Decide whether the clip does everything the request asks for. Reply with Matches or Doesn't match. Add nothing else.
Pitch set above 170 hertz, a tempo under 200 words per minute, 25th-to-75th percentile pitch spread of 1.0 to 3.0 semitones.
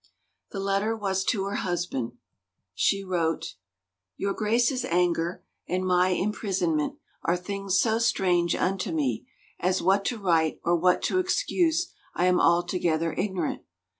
Matches